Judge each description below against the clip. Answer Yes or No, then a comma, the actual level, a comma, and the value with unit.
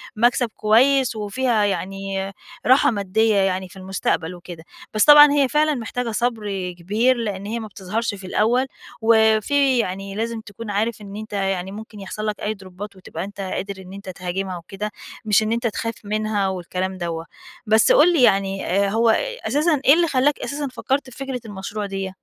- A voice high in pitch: Yes, high, 210 Hz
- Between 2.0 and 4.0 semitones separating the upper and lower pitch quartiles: Yes, average, 3.5 semitones